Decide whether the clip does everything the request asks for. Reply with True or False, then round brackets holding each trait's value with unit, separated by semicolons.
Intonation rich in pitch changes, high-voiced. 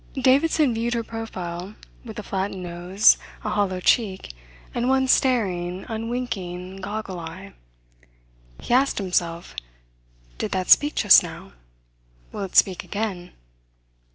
False (4.5 semitones; 200 Hz)